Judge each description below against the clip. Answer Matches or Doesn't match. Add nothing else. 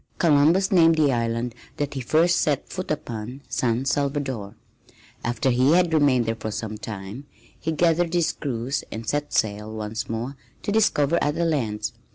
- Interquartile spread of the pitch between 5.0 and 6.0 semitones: Matches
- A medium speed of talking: Matches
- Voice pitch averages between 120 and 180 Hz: Matches